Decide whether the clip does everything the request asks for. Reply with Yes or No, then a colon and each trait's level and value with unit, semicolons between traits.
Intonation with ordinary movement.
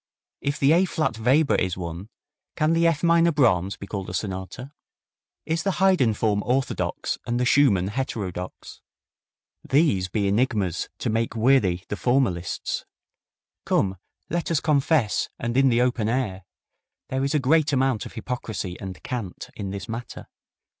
No: wide, 6.4 semitones